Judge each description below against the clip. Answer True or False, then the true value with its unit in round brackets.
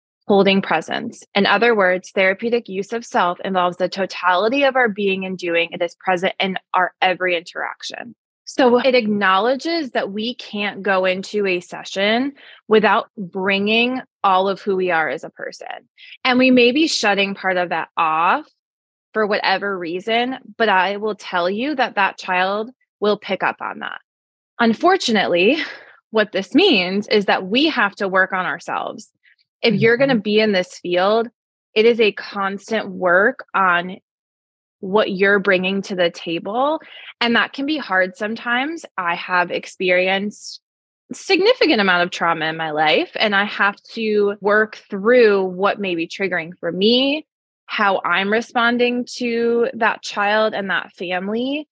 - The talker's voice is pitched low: False (205 Hz)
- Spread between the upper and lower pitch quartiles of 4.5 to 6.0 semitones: False (4.1 semitones)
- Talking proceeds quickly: False (160 wpm)